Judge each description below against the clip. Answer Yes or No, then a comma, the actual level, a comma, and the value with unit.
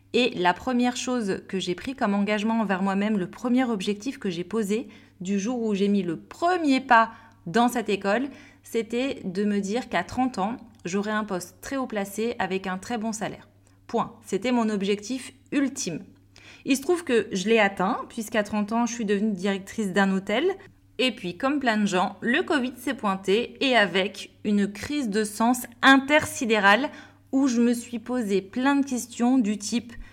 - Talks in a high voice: Yes, high, 225 Hz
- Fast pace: No, average, 185 wpm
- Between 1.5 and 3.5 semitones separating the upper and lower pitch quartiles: No, average, 4.1 semitones